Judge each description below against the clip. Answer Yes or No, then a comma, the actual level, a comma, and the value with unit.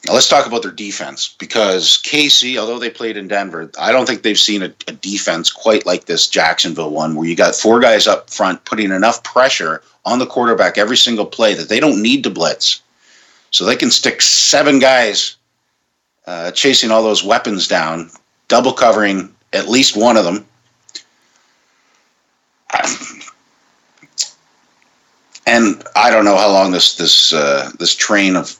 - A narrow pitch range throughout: No, average, 4.7 semitones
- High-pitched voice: No, low, 110 Hz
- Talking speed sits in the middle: Yes, average, 165 wpm